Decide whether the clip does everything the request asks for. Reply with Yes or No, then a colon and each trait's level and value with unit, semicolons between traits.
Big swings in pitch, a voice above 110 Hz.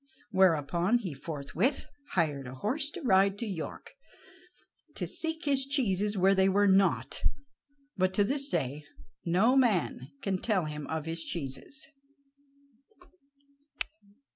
Yes: wide, 6.6 semitones; high, 190 Hz